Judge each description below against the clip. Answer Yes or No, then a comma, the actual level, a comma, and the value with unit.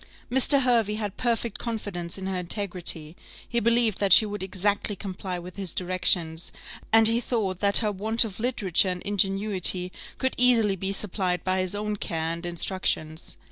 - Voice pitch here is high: Yes, high, 195 Hz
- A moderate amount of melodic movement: Yes, average, 3.3 semitones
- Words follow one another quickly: No, average, 170 wpm